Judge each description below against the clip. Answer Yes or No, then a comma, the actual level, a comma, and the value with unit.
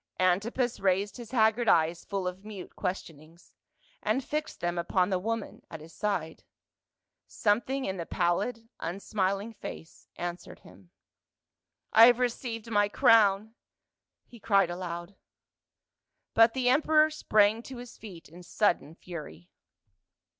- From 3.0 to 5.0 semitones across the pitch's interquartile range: Yes, average, 4.5 semitones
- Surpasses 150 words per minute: No, slow, 135 wpm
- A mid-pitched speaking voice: No, high, 200 Hz